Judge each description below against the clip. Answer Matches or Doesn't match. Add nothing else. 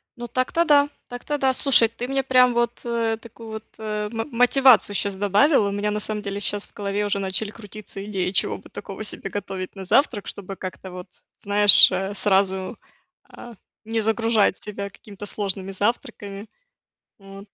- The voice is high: Matches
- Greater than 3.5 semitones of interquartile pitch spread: Doesn't match